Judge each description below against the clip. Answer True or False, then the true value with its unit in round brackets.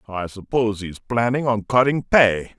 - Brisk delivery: False (185 wpm)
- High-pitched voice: False (115 Hz)